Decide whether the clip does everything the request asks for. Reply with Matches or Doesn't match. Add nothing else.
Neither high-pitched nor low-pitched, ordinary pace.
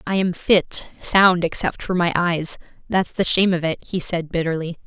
Matches